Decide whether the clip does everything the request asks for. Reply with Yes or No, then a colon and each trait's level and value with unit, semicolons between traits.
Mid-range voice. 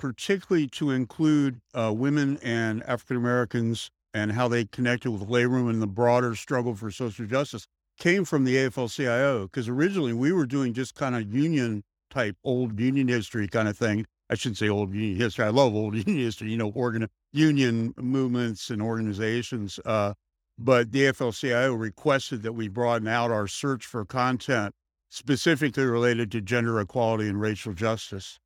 No: low, 120 Hz